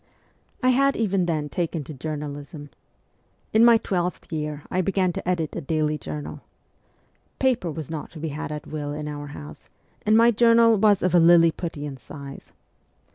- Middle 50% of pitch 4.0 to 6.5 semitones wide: Yes, average, 4.7 semitones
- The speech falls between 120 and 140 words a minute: No, average, 170 wpm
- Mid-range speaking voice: Yes, medium, 160 Hz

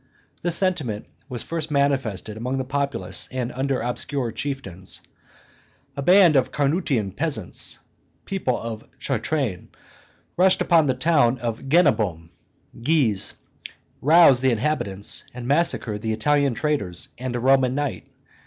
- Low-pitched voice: Yes, low, 130 Hz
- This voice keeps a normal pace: No, slow, 130 wpm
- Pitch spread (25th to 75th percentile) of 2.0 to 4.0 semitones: No, average, 4.5 semitones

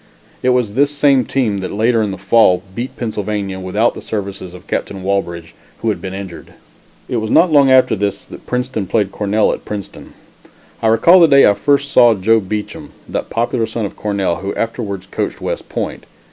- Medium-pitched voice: No, low, 105 Hz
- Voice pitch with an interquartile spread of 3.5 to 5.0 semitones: Yes, average, 4.1 semitones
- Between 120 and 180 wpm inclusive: No, average, 195 wpm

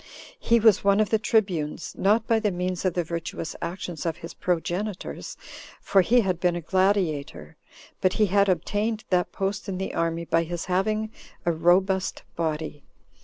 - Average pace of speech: Yes, average, 170 wpm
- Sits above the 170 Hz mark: Yes, medium, 185 Hz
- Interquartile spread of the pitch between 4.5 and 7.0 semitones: No, average, 3.4 semitones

